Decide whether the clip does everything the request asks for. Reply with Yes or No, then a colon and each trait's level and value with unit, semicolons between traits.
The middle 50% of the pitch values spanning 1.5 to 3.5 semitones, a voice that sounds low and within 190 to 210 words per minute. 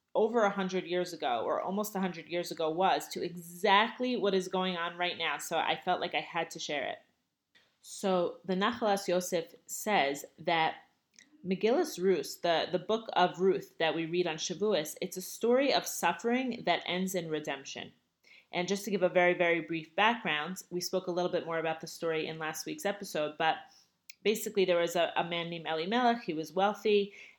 No: average, 3.1 semitones; medium, 180 Hz; average, 195 wpm